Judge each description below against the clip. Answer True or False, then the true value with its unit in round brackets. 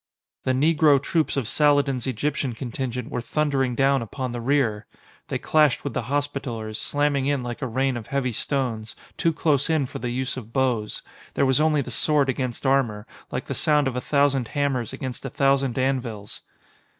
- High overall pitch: False (135 Hz)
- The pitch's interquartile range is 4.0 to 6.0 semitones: False (2.8 semitones)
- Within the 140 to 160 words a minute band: False (185 wpm)